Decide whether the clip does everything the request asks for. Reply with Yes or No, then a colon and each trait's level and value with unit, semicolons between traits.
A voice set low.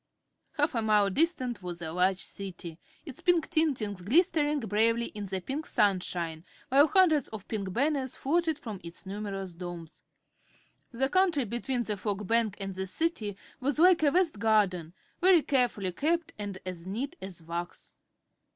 No: high, 220 Hz